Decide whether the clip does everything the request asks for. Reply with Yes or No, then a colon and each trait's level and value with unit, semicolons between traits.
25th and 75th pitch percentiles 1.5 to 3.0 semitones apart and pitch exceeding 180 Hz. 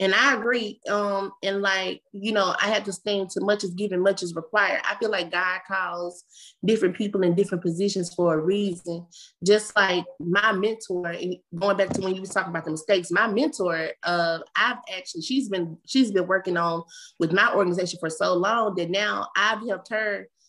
Yes: average, 2.7 semitones; high, 190 Hz